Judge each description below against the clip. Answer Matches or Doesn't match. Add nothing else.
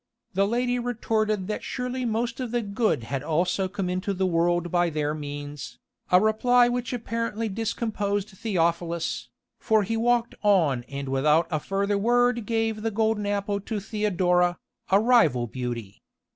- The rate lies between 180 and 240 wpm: Doesn't match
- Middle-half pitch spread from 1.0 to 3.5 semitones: Doesn't match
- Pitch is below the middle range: Doesn't match